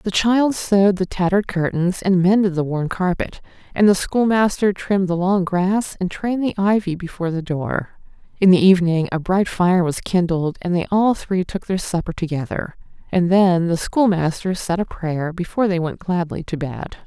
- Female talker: Yes, female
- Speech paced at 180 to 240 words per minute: Yes, average, 190 wpm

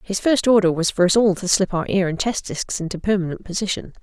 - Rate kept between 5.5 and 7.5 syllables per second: Yes, 6.0 syllables/s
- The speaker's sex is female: Yes, female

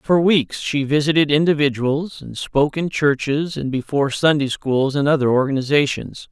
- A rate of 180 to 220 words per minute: No, average, 150 wpm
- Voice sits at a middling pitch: Yes, medium, 145 Hz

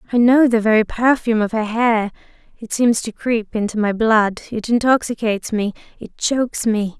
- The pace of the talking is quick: No, average, 180 wpm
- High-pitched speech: Yes, high, 225 Hz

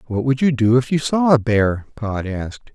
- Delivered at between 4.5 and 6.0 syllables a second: Yes, 4.8 syllables/s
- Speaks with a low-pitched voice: Yes, low, 120 Hz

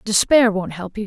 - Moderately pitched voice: No, high, 205 Hz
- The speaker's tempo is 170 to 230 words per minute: Yes, fast, 225 wpm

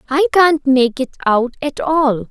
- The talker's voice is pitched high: Yes, very high, 290 Hz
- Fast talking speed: No, average, 185 wpm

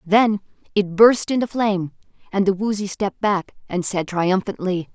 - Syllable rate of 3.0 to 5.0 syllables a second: Yes, 4.8 syllables/s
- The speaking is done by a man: No, female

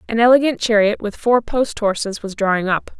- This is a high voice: Yes, high, 220 Hz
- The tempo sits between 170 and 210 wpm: Yes, average, 200 wpm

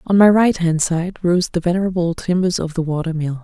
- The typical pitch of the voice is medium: Yes, medium, 175 Hz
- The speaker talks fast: Yes, fast, 225 wpm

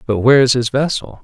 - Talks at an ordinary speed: No, fast, 245 wpm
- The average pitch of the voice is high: No, low, 125 Hz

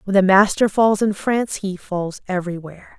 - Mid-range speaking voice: No, high, 195 Hz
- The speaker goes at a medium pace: Yes, average, 180 wpm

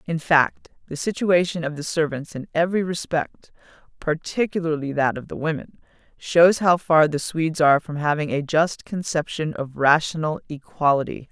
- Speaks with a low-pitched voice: No, medium, 160 Hz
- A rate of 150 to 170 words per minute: Yes, average, 155 wpm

